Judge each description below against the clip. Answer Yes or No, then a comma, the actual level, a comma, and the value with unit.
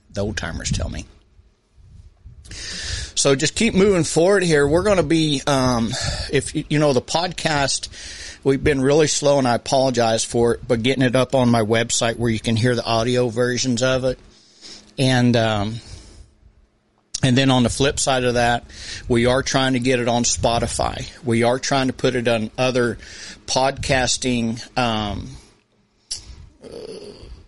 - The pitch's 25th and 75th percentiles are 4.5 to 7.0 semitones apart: No, average, 2.9 semitones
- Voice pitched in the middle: No, low, 125 Hz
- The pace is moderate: Yes, average, 165 wpm